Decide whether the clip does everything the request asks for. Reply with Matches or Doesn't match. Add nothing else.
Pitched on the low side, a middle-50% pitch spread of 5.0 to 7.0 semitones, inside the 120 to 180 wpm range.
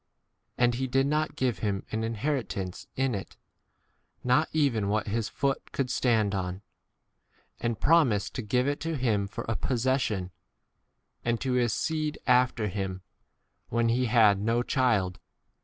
Doesn't match